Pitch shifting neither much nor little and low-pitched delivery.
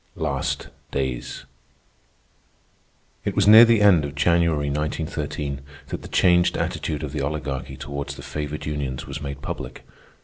No: narrow, 2.3 semitones; very low, 75 Hz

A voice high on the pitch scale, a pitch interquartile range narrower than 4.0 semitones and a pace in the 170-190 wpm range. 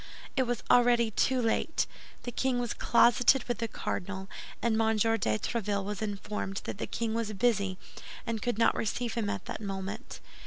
Yes: high, 225 Hz; average, 2.8 semitones; average, 180 wpm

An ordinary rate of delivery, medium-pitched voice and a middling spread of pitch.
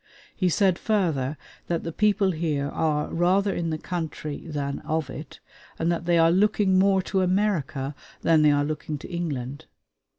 Yes: average, 170 wpm; medium, 165 Hz; average, 3.9 semitones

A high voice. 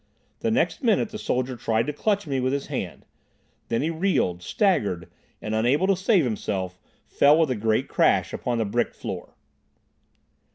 No: low, 130 Hz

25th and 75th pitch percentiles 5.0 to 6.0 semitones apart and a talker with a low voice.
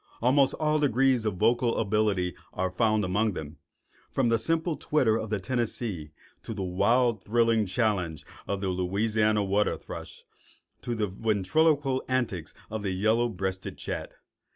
No: average, 3.9 semitones; low, 110 Hz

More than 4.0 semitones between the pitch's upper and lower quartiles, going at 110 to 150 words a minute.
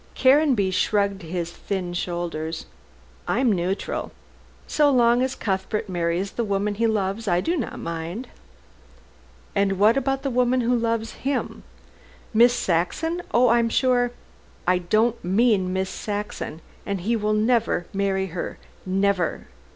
Yes: average, 4.5 semitones; average, 145 wpm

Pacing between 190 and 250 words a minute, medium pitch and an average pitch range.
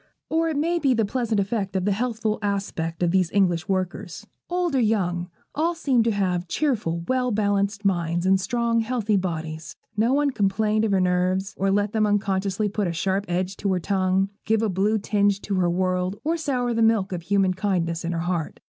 No: fast, 205 wpm; high, 200 Hz; average, 3.4 semitones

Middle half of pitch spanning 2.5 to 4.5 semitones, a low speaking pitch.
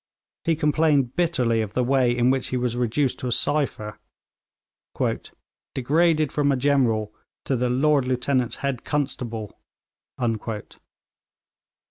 Yes: average, 3.1 semitones; low, 130 Hz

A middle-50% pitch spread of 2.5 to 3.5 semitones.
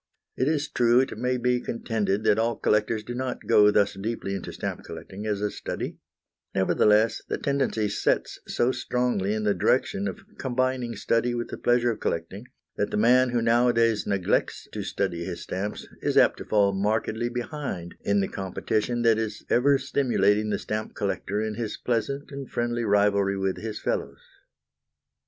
Yes: average, 3.1 semitones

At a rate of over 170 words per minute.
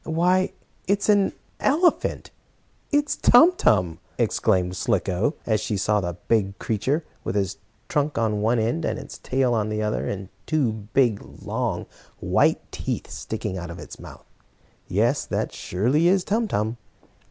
No: average, 155 wpm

